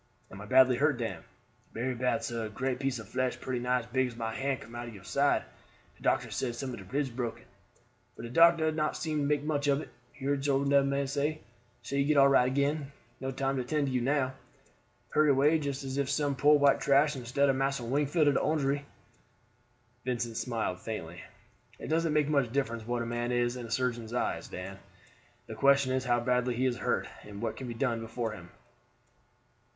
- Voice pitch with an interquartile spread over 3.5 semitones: No, average, 3.0 semitones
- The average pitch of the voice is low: Yes, low, 130 Hz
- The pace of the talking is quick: Yes, fast, 220 wpm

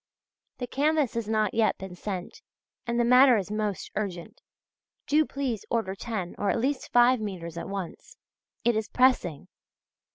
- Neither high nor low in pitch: No, high, 220 Hz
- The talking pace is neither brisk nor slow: Yes, average, 160 wpm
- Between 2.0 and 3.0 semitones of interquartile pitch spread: No, average, 4.3 semitones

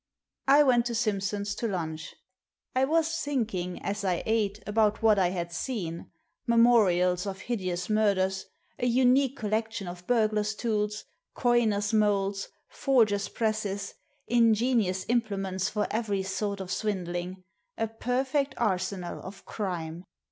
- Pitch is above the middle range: Yes, high, 210 Hz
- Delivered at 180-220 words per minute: No, slow, 135 wpm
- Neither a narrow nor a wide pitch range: Yes, average, 3.6 semitones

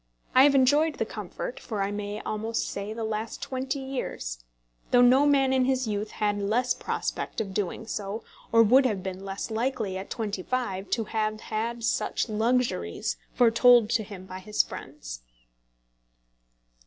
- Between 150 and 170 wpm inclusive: Yes, average, 165 wpm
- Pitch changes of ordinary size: Yes, average, 3.8 semitones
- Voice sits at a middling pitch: No, high, 220 Hz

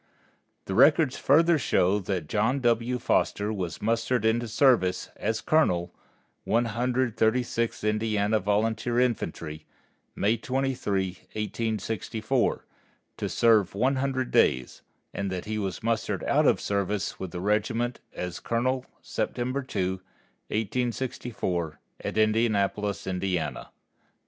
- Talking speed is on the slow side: Yes, slow, 120 wpm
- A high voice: No, low, 110 Hz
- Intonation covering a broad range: No, average, 3.7 semitones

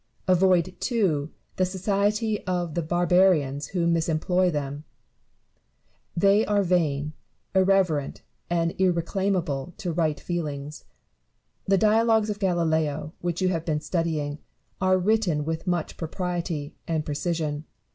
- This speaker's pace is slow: Yes, slow, 120 wpm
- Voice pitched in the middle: Yes, medium, 175 Hz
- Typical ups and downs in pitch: Yes, average, 3.4 semitones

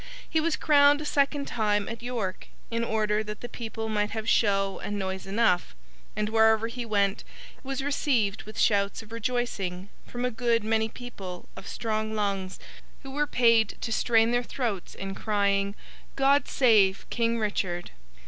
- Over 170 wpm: No, average, 160 wpm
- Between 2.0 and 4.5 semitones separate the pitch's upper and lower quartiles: Yes, average, 3.2 semitones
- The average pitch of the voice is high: Yes, high, 220 Hz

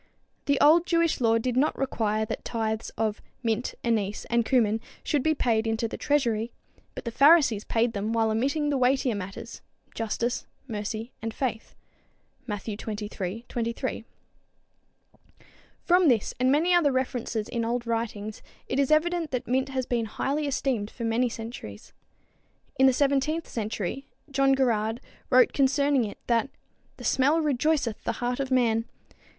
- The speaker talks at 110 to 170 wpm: Yes, average, 155 wpm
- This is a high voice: Yes, high, 240 Hz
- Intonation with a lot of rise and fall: No, average, 3.6 semitones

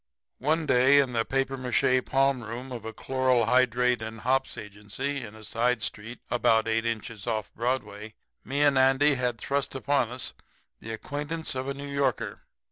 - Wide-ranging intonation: No, average, 3.0 semitones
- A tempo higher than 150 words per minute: Yes, average, 175 wpm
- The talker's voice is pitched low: Yes, low, 125 Hz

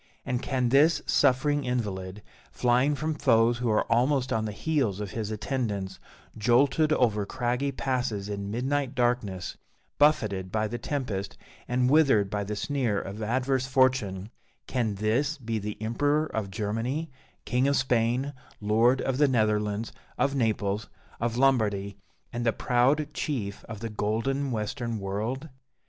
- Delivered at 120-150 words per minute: Yes, average, 145 wpm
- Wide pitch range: No, average, 4.1 semitones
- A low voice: Yes, low, 120 Hz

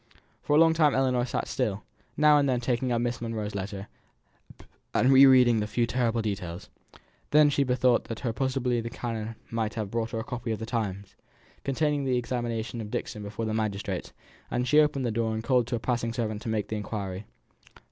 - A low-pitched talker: Yes, low, 115 Hz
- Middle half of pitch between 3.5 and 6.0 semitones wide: No, average, 2.8 semitones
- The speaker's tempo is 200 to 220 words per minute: Yes, fast, 205 wpm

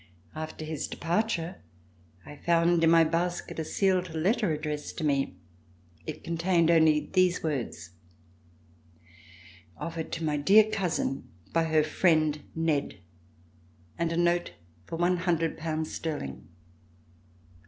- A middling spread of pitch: No, narrow, 1.9 semitones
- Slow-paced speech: Yes, slow, 125 wpm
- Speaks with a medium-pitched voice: Yes, medium, 165 Hz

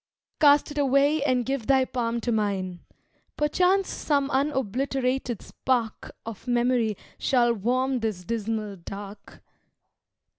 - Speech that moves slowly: Yes, slow, 115 wpm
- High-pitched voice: Yes, very high, 250 Hz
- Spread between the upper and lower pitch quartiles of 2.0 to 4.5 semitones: Yes, average, 3.8 semitones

